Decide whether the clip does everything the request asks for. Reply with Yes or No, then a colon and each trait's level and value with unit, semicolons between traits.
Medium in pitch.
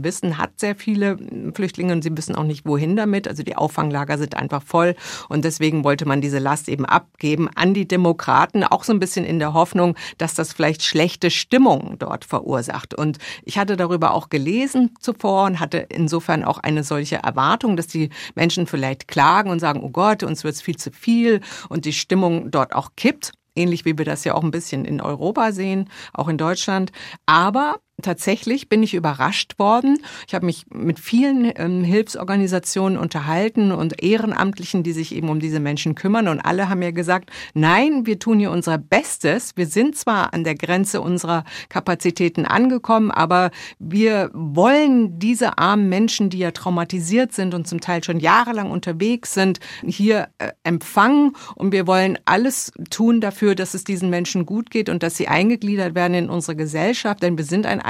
Yes: medium, 180 Hz